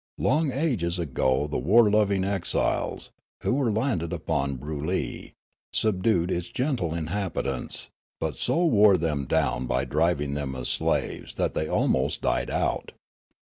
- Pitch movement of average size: No, wide, 6.7 semitones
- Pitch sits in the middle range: No, very low, 85 Hz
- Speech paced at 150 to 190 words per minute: No, average, 140 wpm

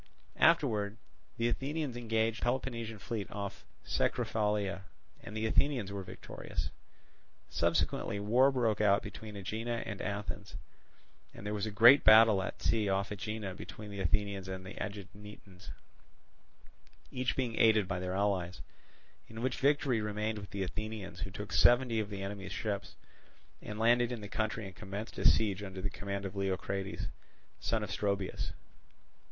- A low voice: Yes, low, 105 Hz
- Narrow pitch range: Yes, narrow, 2.3 semitones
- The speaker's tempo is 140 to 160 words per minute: Yes, average, 150 wpm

